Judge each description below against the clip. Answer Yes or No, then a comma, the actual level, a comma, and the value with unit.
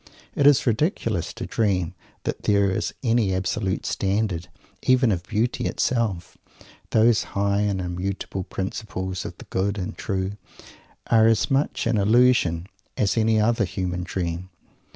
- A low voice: Yes, low, 100 Hz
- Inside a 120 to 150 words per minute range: Yes, average, 140 wpm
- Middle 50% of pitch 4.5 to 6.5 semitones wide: No, average, 3.4 semitones